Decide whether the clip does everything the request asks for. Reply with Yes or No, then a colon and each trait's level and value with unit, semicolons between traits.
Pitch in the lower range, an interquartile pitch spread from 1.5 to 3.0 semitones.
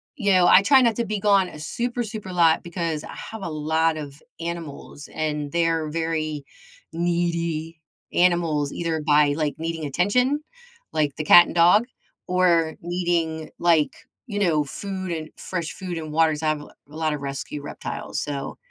No: medium, 165 Hz; average, 2.7 semitones